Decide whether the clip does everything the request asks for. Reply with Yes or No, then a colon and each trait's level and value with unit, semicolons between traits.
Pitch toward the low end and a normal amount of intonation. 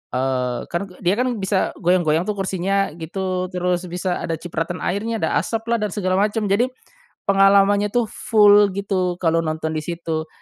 No: medium, 185 Hz; average, 3.0 semitones